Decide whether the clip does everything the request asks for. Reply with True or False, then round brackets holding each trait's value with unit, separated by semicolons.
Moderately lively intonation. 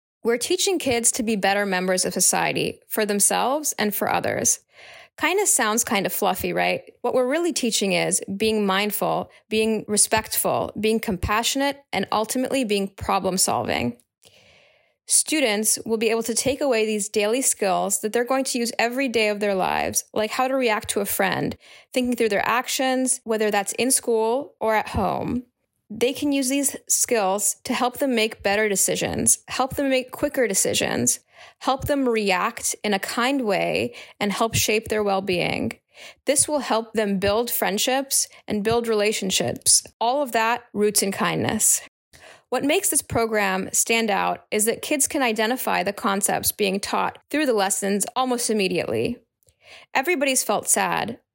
True (4.0 semitones)